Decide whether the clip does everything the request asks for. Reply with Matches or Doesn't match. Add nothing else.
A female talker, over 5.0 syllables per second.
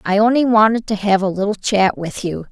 Matches